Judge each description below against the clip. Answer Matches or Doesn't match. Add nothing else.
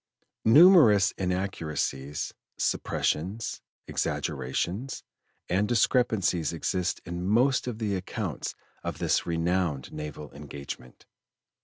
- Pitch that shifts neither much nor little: Doesn't match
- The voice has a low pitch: Matches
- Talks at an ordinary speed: Doesn't match